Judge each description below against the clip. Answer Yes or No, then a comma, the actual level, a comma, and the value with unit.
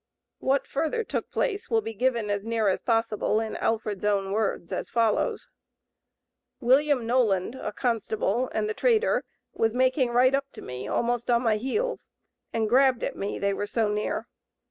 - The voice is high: Yes, high, 230 Hz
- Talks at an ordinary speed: Yes, average, 170 wpm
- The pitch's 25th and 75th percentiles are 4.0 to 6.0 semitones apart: No, average, 3.4 semitones